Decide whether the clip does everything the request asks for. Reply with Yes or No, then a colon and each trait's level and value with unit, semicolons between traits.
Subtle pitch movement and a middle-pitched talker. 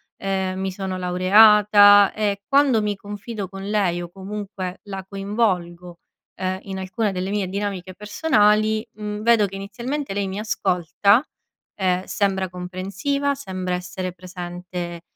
No: narrow, 2.2 semitones; high, 195 Hz